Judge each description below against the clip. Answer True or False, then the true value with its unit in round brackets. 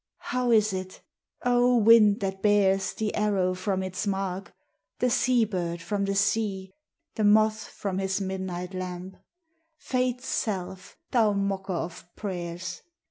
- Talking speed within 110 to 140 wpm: True (135 wpm)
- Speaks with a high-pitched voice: True (195 Hz)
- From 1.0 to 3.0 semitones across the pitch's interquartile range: True (2.5 semitones)